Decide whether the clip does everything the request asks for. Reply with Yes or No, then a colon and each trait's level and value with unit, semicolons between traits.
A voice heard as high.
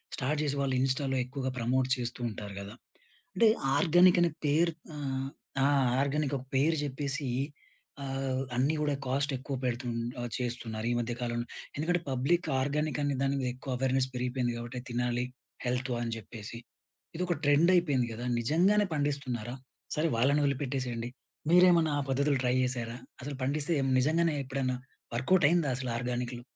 No: low, 135 Hz